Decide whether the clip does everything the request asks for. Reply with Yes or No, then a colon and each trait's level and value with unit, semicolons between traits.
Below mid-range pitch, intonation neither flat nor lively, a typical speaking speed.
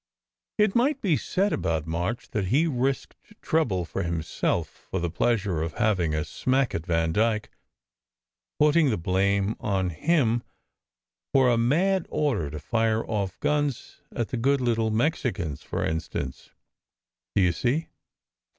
No: low, 110 Hz; wide, 8.0 semitones; average, 145 wpm